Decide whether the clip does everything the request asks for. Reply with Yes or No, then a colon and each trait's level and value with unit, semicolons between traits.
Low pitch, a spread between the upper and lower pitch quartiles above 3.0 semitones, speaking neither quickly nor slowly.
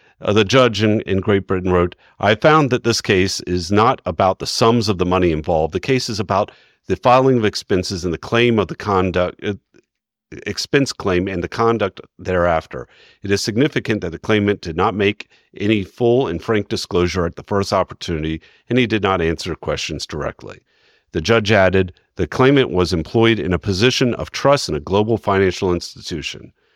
Yes: low, 100 Hz; average, 4.1 semitones; average, 190 wpm